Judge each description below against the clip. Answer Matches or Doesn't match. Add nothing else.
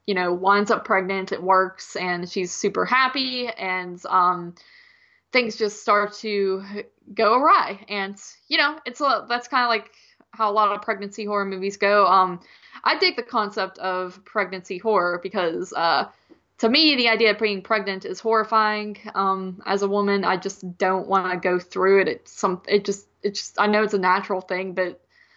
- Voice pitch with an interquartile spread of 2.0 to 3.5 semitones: Matches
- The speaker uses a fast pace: Doesn't match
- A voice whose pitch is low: Doesn't match